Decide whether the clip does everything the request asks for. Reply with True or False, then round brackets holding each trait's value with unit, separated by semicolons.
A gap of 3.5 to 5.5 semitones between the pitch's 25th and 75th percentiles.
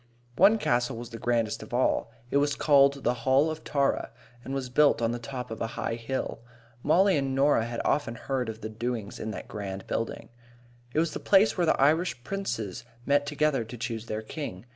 True (4.0 semitones)